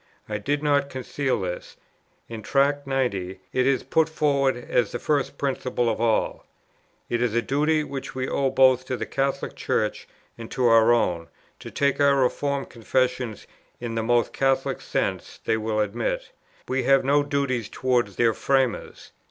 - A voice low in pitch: Yes, low, 130 Hz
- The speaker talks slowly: No, average, 170 wpm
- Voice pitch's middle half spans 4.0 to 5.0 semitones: No, average, 3.2 semitones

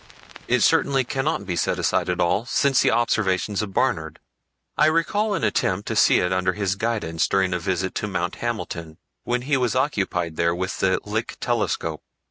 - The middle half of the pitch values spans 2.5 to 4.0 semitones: No, average, 5.3 semitones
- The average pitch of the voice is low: Yes, low, 100 Hz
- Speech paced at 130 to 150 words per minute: No, average, 185 wpm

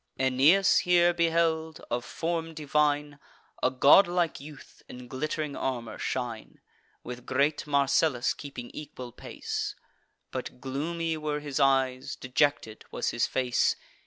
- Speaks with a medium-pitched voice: Yes, medium, 145 Hz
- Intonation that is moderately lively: Yes, average, 3.8 semitones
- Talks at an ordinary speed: No, slow, 120 wpm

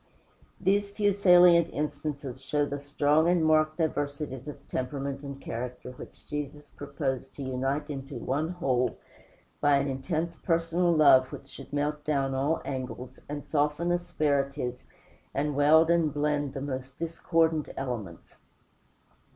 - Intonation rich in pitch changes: No, average, 2.8 semitones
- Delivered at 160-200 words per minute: No, slow, 135 wpm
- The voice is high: No, medium, 145 Hz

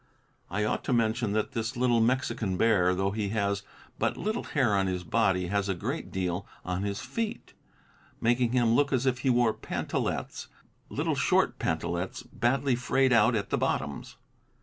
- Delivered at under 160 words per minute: No, average, 170 wpm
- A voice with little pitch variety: No, average, 4.2 semitones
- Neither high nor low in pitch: No, low, 110 Hz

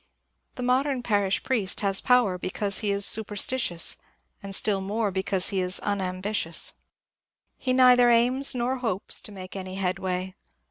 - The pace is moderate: Yes, average, 170 wpm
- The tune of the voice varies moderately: Yes, average, 4.2 semitones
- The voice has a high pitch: Yes, high, 200 Hz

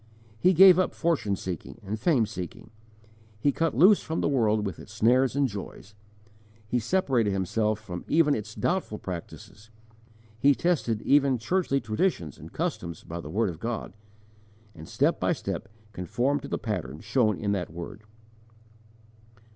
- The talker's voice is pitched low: Yes, low, 110 Hz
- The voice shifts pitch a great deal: Yes, wide, 6.1 semitones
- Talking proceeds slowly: No, average, 155 wpm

